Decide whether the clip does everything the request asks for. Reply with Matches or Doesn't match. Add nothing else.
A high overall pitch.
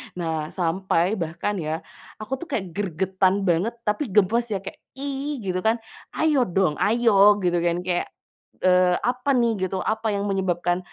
Matches